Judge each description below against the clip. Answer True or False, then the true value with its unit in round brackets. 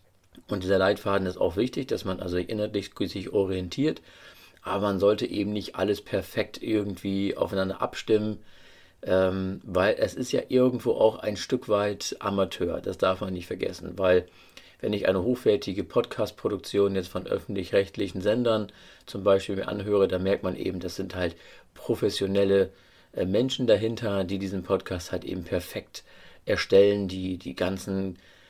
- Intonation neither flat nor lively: False (1.7 semitones)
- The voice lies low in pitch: True (95 Hz)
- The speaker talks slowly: False (150 wpm)